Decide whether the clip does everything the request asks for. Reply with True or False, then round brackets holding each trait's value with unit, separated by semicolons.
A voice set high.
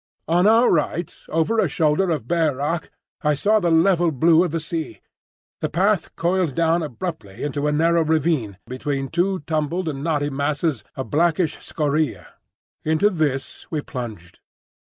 False (160 Hz)